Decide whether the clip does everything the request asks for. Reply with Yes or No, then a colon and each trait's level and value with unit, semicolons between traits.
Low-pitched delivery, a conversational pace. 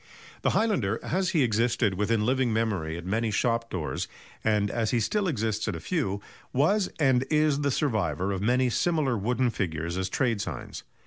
Yes: low, 115 Hz; average, 180 wpm